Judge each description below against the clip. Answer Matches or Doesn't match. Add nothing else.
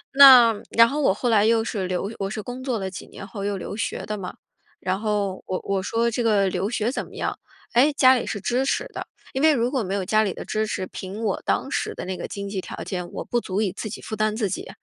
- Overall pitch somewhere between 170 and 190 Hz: Doesn't match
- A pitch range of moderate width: Matches